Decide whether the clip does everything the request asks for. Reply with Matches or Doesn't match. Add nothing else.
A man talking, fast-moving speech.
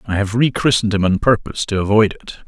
Matches